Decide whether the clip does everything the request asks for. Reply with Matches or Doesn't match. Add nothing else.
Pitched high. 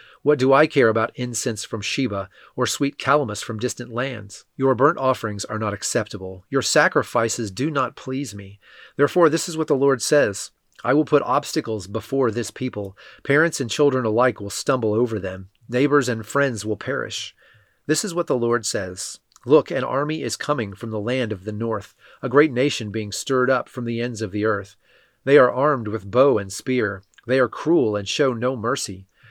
Doesn't match